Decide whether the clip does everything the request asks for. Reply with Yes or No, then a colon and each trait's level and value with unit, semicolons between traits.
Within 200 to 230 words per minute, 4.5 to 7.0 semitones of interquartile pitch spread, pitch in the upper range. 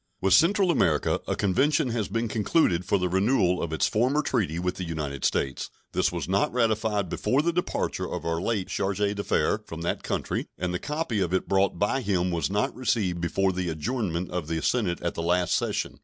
No: fast, 205 wpm; average, 4.8 semitones; very low, 95 Hz